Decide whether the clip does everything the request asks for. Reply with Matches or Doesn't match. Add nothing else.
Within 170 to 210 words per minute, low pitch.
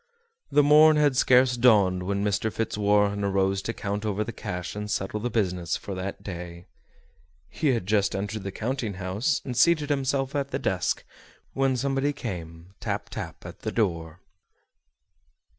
Doesn't match